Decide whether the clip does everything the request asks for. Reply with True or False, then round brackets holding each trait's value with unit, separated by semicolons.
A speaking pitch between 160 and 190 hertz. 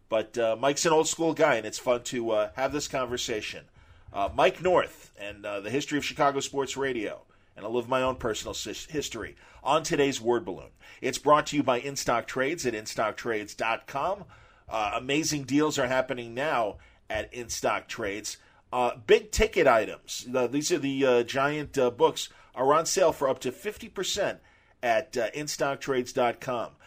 False (135 Hz)